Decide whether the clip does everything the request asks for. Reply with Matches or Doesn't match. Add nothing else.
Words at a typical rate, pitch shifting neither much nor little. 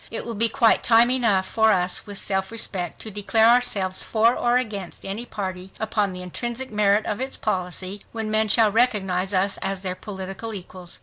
Matches